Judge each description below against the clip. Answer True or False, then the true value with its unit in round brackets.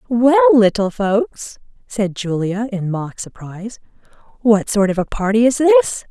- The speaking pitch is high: True (220 Hz)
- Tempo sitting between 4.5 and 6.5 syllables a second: False (4.2 syllables/s)